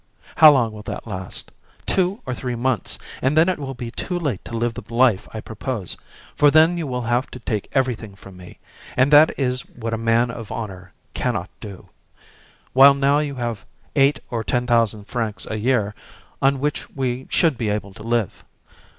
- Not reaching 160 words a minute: No, average, 195 wpm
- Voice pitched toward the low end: Yes, low, 120 Hz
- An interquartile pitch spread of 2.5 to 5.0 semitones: Yes, average, 3.8 semitones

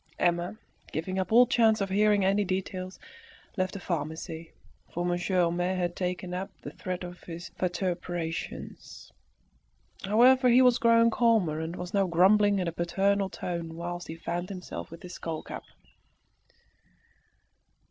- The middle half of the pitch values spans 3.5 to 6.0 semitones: No, narrow, 2.6 semitones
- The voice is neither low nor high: Yes, medium, 180 Hz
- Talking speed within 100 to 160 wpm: Yes, average, 145 wpm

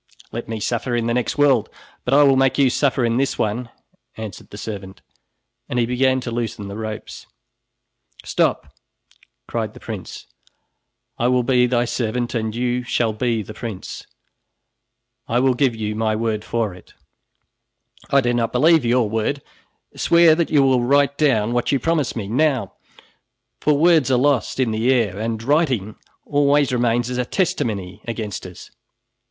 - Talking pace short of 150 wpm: No, average, 170 wpm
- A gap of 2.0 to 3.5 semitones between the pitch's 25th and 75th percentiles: Yes, average, 3.2 semitones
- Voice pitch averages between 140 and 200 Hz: No, low, 120 Hz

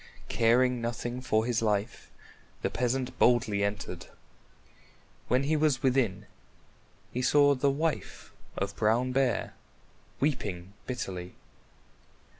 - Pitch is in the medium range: No, low, 120 Hz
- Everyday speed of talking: No, slow, 105 wpm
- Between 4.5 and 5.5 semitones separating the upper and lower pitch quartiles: No, average, 3.7 semitones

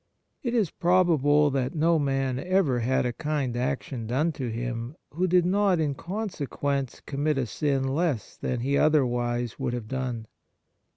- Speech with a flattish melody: No, average, 4.5 semitones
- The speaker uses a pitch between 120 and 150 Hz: Yes, medium, 140 Hz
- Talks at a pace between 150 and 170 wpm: Yes, average, 160 wpm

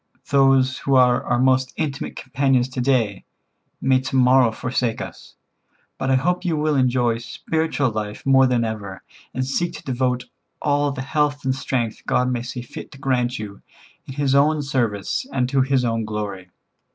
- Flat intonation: Yes, narrow, 2.2 semitones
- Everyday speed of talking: Yes, average, 175 wpm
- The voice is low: Yes, low, 130 Hz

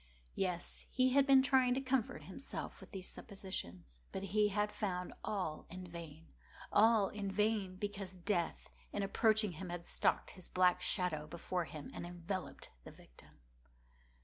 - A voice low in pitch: No, high, 190 Hz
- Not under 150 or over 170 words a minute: Yes, average, 160 wpm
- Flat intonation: No, average, 3.4 semitones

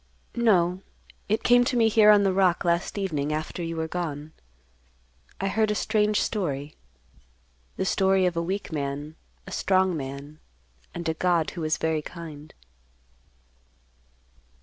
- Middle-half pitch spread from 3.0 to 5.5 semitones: Yes, average, 4.0 semitones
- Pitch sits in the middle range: Yes, medium, 175 Hz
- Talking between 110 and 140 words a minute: No, average, 150 wpm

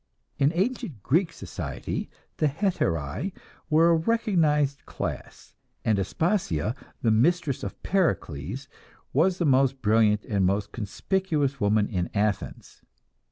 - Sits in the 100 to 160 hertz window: Yes, low, 135 Hz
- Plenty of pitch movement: Yes, wide, 8.5 semitones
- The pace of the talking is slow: Yes, slow, 115 wpm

